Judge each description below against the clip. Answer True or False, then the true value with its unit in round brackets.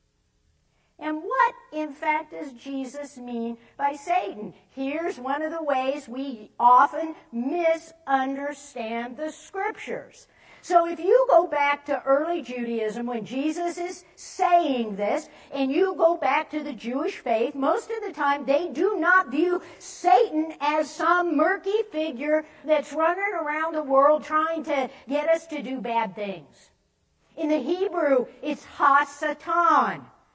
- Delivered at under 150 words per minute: True (140 wpm)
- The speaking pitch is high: True (305 Hz)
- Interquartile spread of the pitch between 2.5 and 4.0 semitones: True (3.7 semitones)